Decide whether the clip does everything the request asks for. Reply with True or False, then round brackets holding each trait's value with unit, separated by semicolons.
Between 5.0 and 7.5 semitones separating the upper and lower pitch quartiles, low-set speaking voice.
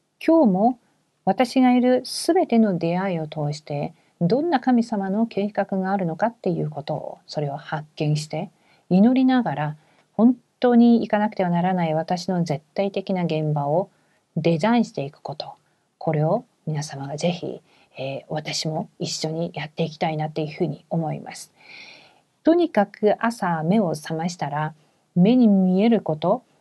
False (5.6 semitones; 180 Hz)